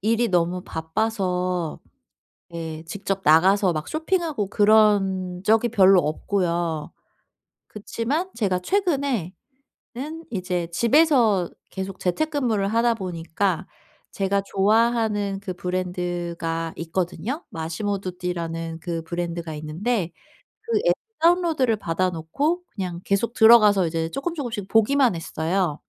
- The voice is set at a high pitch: Yes, high, 195 Hz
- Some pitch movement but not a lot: Yes, average, 5.0 semitones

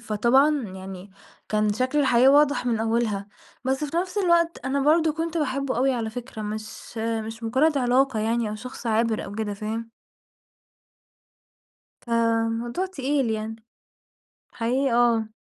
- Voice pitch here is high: Yes, high, 235 Hz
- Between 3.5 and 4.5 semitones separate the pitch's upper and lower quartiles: Yes, average, 3.8 semitones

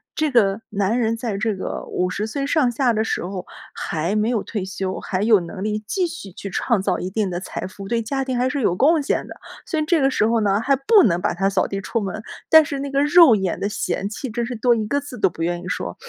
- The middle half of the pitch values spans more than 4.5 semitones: Yes, wide, 5.5 semitones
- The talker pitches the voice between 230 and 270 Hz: No, high, 220 Hz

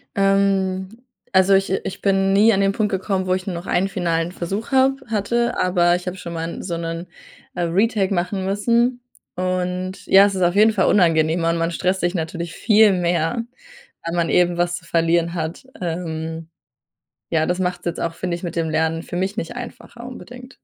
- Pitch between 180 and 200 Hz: Yes, medium, 185 Hz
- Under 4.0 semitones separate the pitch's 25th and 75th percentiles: Yes, average, 2.7 semitones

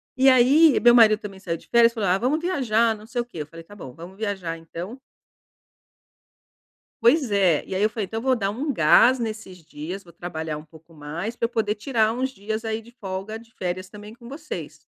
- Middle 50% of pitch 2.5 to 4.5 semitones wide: No, average, 4.9 semitones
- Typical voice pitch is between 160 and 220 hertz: Yes, high, 215 Hz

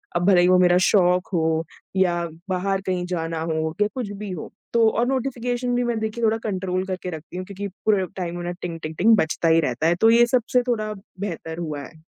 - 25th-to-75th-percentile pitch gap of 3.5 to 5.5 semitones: Yes, average, 4.5 semitones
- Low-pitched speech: No, medium, 185 Hz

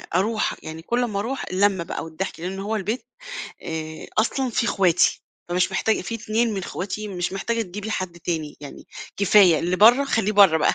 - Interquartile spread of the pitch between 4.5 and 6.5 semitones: No, average, 3.8 semitones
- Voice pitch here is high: Yes, high, 195 Hz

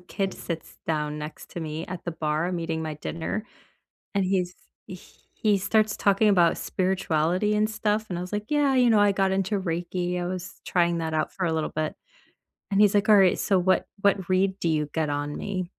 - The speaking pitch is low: No, medium, 185 Hz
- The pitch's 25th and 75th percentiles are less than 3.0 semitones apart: No, average, 3.6 semitones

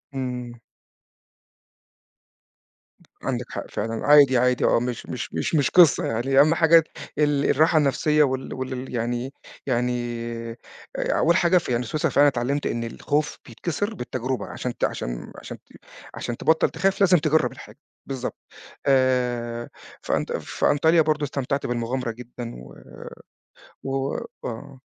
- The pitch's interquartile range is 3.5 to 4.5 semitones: Yes, average, 3.8 semitones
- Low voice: Yes, low, 130 Hz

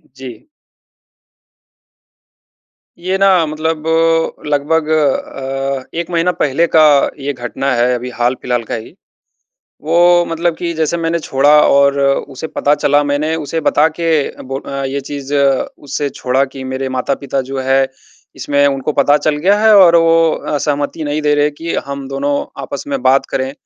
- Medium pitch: Yes, medium, 145 Hz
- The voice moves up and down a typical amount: Yes, average, 3.1 semitones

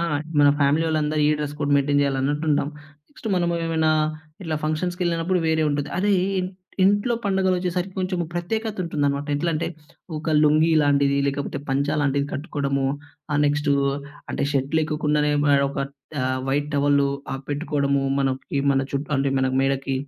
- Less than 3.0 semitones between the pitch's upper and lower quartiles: No, average, 3.3 semitones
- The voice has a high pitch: No, medium, 150 Hz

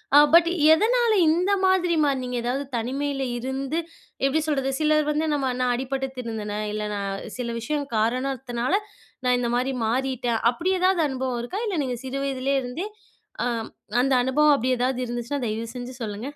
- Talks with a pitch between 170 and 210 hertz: No, very high, 260 Hz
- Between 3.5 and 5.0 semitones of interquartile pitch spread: No, average, 3.1 semitones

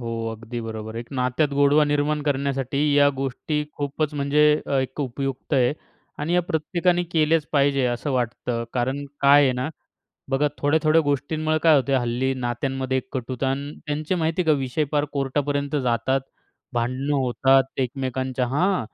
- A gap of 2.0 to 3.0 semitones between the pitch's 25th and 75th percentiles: Yes, narrow, 2.6 semitones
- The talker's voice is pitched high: No, medium, 140 Hz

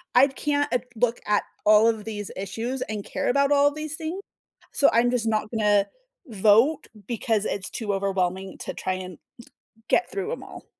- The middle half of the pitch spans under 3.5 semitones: No, average, 5.3 semitones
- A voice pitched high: Yes, high, 225 Hz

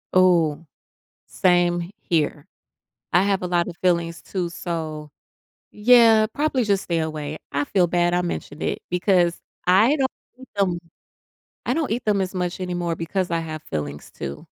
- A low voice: No, medium, 175 Hz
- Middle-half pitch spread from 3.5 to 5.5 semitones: No, average, 2.8 semitones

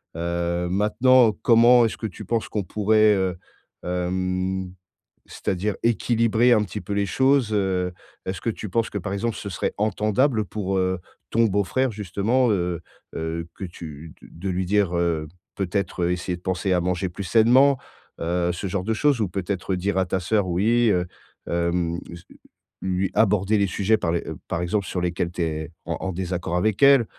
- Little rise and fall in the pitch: No, average, 3.5 semitones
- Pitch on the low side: Yes, very low, 95 Hz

